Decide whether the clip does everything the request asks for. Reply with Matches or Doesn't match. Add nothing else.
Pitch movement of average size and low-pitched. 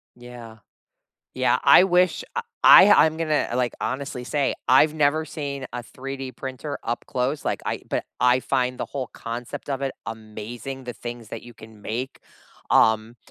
Matches